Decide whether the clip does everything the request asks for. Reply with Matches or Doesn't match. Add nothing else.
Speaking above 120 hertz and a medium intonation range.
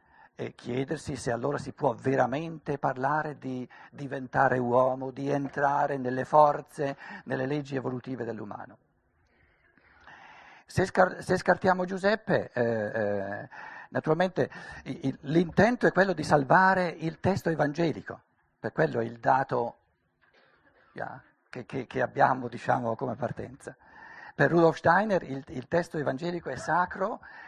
Matches